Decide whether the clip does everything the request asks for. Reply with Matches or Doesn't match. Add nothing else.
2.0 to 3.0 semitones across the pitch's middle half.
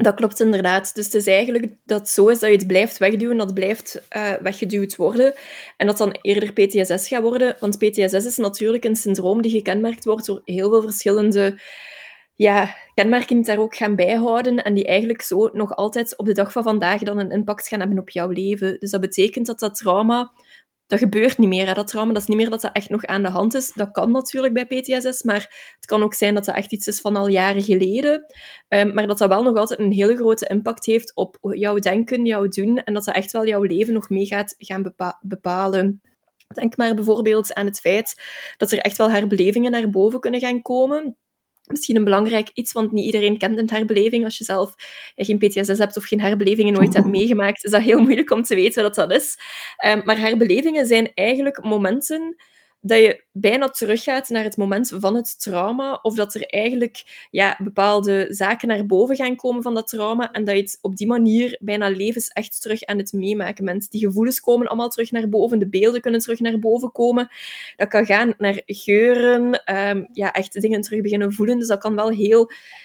Matches